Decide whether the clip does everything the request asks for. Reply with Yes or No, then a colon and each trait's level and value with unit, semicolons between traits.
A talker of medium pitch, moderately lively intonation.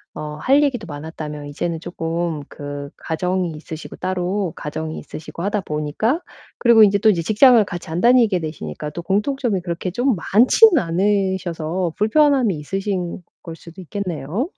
Yes: medium, 180 Hz; average, 4.8 semitones